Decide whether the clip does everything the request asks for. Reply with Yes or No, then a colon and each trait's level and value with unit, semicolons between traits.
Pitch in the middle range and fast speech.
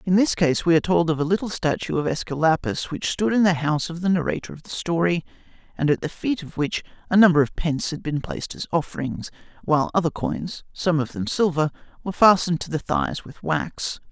Yes: medium, 165 Hz; fast, 220 wpm